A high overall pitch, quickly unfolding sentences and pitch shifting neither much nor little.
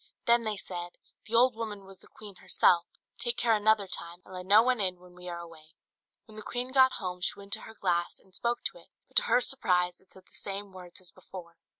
Yes: high, 195 Hz; fast, 245 wpm; average, 3.8 semitones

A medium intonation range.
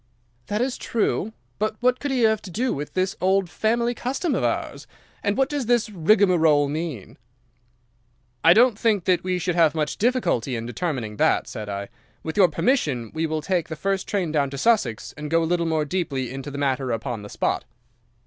No: wide, 6.9 semitones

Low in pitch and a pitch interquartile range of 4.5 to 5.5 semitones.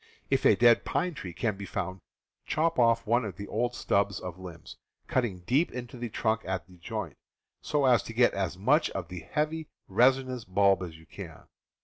Yes: low, 110 Hz; average, 5.2 semitones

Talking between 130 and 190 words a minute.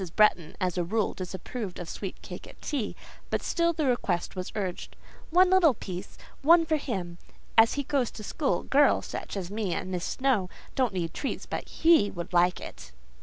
Yes: average, 170 wpm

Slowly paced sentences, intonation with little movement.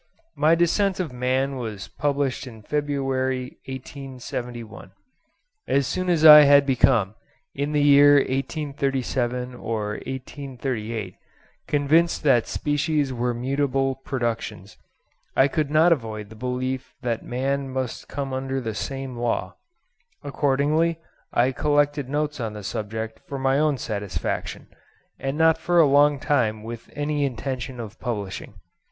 No: slow, 130 wpm; average, 3.3 semitones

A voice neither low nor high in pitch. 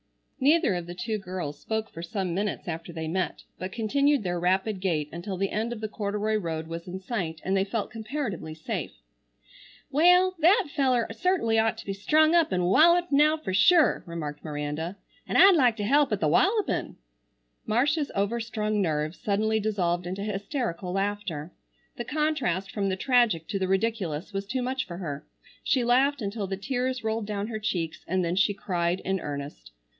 No: high, 205 Hz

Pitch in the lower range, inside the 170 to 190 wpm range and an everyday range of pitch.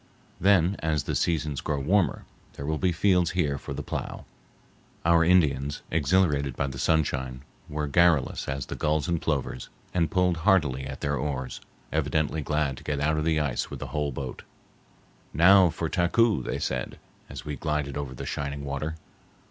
Yes: very low, 75 Hz; average, 175 wpm; average, 3.3 semitones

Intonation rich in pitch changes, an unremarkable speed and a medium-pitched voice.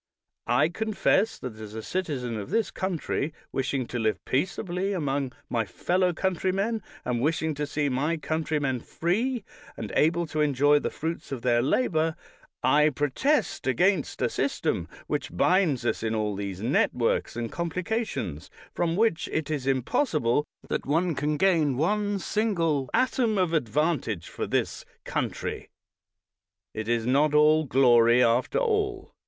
Yes: wide, 6.4 semitones; average, 150 wpm; medium, 150 Hz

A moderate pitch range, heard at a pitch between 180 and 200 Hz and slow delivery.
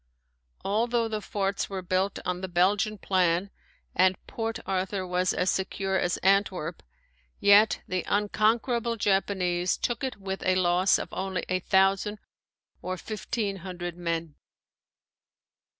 No: narrow, 2.2 semitones; high, 190 Hz; slow, 130 wpm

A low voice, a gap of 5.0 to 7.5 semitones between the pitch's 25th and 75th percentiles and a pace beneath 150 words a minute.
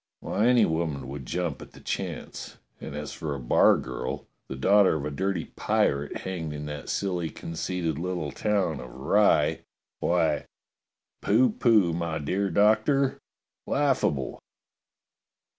Yes: very low, 85 Hz; wide, 5.5 semitones; average, 140 wpm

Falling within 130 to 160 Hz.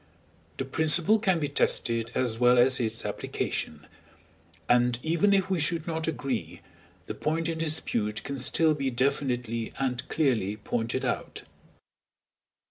Yes: low, 135 Hz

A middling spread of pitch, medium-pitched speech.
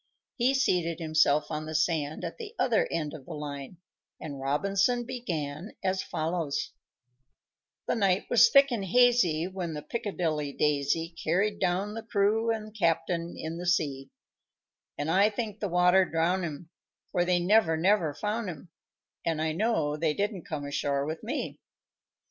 Yes: average, 4.8 semitones; medium, 175 Hz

